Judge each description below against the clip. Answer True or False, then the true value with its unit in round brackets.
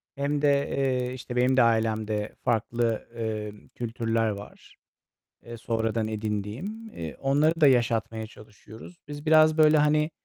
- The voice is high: False (115 Hz)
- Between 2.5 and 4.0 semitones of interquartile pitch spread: False (4.8 semitones)